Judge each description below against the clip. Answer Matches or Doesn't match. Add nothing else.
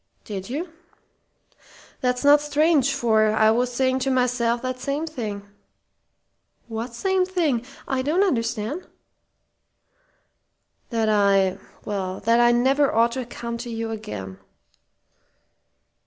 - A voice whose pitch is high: Matches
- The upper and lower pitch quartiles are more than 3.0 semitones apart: Matches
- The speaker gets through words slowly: Matches